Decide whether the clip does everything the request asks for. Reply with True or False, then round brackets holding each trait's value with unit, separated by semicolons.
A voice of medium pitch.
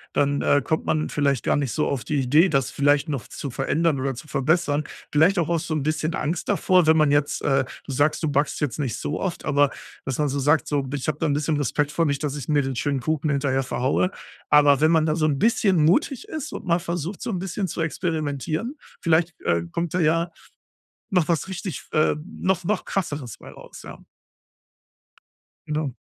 True (150 Hz)